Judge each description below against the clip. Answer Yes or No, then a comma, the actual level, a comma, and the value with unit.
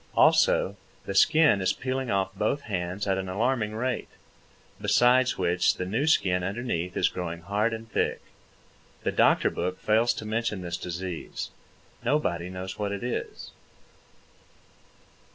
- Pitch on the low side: Yes, low, 100 Hz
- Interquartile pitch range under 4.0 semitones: No, average, 4.5 semitones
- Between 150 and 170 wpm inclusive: No, average, 140 wpm